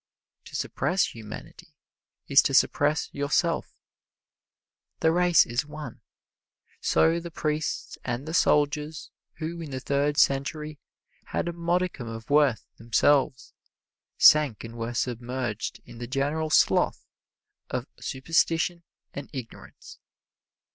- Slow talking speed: Yes, slow, 115 wpm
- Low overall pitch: No, medium, 145 Hz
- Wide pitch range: No, average, 4.1 semitones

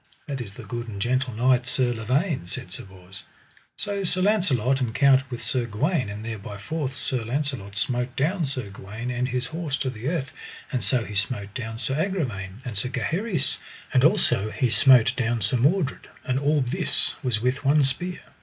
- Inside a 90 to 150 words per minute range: No, average, 190 wpm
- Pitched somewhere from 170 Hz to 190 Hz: No, low, 125 Hz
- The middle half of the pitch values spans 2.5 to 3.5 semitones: No, average, 4.1 semitones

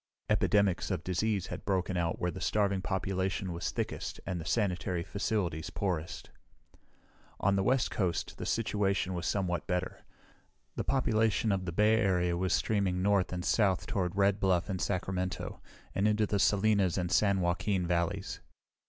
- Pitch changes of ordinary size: No, narrow, 2.3 semitones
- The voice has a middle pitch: No, very low, 95 Hz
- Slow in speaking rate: No, average, 160 wpm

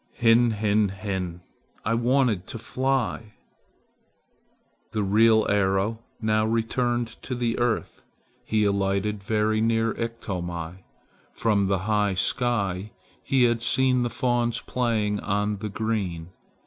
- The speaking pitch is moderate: No, low, 110 Hz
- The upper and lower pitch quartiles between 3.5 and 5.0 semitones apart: No, average, 2.7 semitones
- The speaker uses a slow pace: Yes, slow, 120 wpm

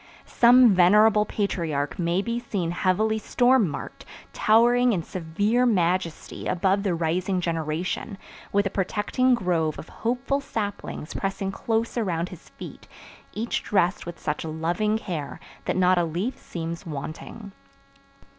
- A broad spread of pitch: No, average, 4.5 semitones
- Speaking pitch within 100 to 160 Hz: No, high, 190 Hz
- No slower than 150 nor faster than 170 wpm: No, slow, 135 wpm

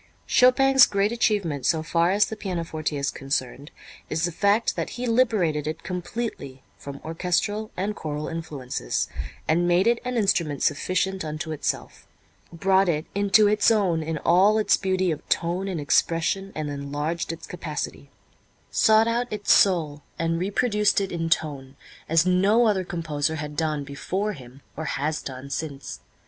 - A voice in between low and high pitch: Yes, medium, 170 Hz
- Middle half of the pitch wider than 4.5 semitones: Yes, average, 4.9 semitones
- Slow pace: No, average, 160 wpm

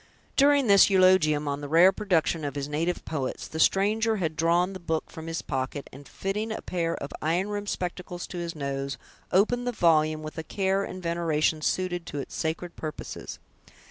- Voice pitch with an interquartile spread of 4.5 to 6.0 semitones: No, average, 3.8 semitones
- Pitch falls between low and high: Yes, medium, 170 Hz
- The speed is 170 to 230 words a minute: Yes, average, 190 wpm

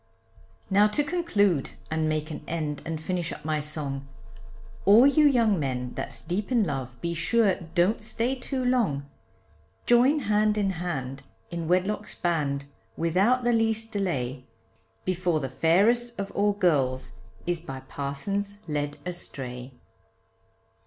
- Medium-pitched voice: Yes, medium, 175 Hz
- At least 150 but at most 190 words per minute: No, average, 140 wpm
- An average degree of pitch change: No, wide, 6.6 semitones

